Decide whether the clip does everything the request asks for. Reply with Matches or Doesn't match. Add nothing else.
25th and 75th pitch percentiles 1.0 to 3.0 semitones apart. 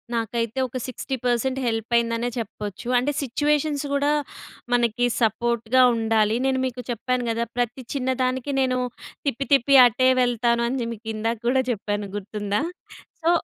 Matches